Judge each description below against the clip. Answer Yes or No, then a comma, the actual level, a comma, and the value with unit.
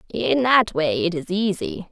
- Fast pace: No, average, 190 wpm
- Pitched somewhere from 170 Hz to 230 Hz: Yes, high, 190 Hz